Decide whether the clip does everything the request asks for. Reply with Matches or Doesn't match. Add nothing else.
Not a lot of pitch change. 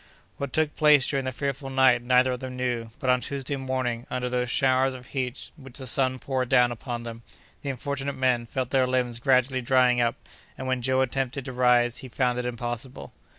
Matches